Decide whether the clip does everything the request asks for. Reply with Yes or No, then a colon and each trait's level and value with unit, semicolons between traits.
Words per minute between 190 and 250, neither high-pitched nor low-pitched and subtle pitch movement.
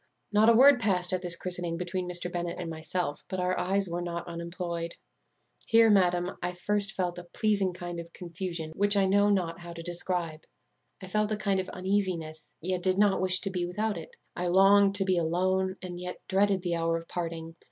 Yes: fast, 205 wpm; medium, 180 Hz; narrow, 2.1 semitones